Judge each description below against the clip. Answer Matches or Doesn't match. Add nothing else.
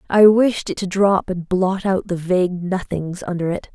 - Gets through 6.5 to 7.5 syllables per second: Doesn't match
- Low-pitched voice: Doesn't match